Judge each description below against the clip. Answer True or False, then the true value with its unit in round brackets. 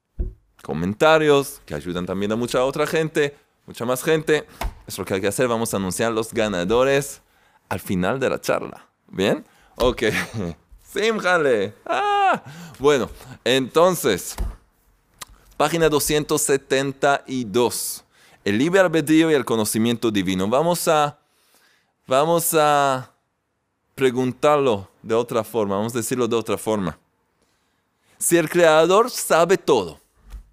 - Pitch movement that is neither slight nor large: False (5.8 semitones)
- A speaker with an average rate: False (120 wpm)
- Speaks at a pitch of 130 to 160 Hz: True (140 Hz)